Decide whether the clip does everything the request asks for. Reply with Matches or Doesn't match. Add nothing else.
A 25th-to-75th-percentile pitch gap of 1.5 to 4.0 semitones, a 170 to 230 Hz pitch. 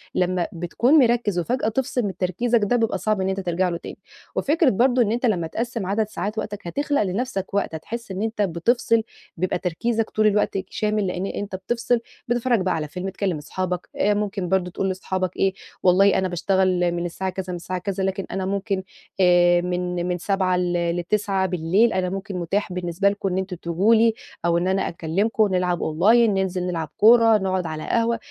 Matches